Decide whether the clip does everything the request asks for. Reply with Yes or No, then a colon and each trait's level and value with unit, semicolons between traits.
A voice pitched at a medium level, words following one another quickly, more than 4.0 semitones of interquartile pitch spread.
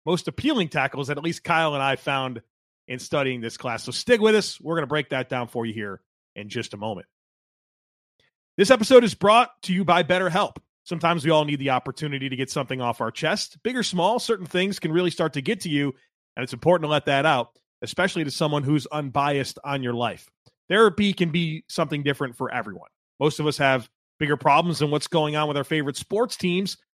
Yes: medium, 150 Hz; fast, 225 wpm; average, 5.0 semitones